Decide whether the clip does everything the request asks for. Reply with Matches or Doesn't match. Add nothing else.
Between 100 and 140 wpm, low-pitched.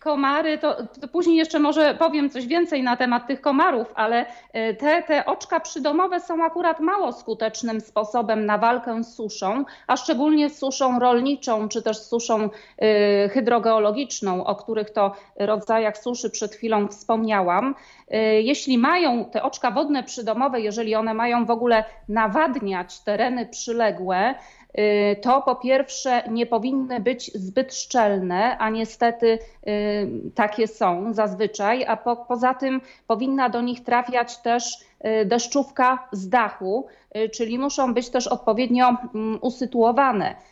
Doesn't match